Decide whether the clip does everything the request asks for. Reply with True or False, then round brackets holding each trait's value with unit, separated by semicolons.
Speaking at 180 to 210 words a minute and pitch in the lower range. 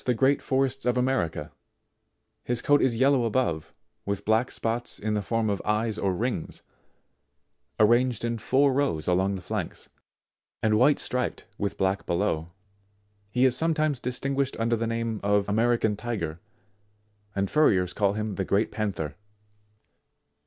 False (145 wpm; 115 Hz)